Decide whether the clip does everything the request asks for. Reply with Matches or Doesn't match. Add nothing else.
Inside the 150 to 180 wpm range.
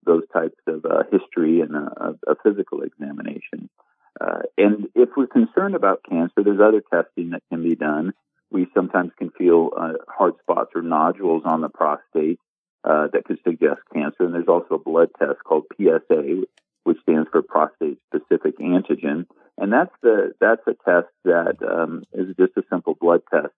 Matches